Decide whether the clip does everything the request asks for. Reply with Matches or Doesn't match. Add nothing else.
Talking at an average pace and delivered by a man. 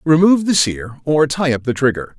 Doesn't match